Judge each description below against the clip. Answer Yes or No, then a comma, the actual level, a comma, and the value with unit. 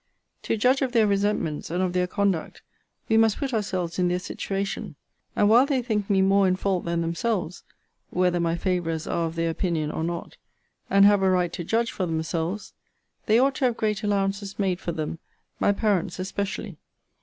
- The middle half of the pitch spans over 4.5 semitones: No, average, 3.4 semitones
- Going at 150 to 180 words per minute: No, average, 190 wpm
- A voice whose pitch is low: No, high, 190 Hz